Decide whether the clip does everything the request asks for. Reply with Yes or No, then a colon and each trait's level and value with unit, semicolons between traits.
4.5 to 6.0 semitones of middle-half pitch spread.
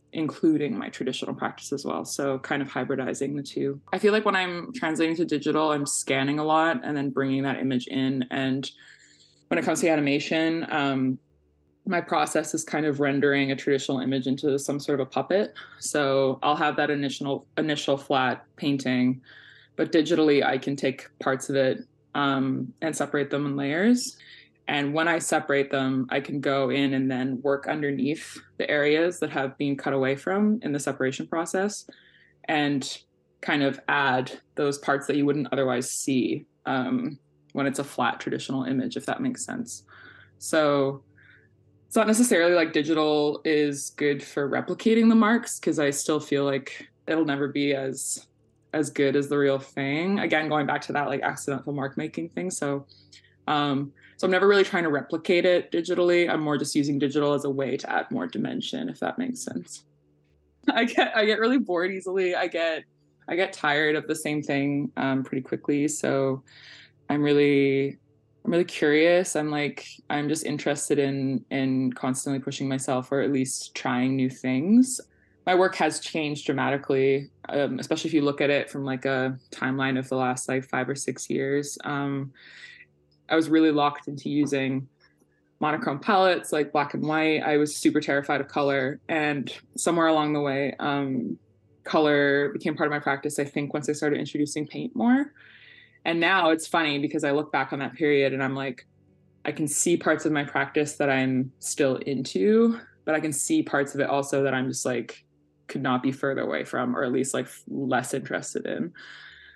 No: narrow, 2.5 semitones